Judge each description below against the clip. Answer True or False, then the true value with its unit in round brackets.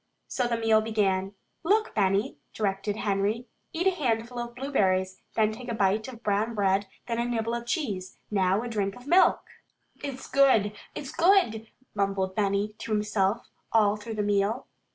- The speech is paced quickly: False (170 wpm)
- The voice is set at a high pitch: True (220 Hz)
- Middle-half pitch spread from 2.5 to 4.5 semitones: True (3.2 semitones)